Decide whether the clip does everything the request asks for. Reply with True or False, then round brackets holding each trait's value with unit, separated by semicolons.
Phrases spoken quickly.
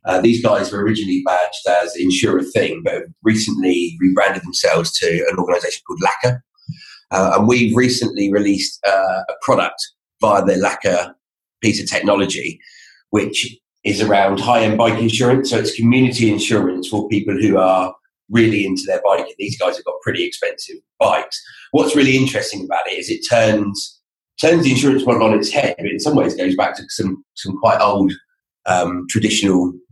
False (170 wpm)